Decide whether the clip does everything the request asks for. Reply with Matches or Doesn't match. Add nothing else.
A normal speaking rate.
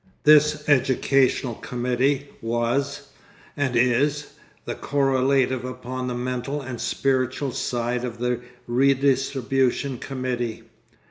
Doesn't match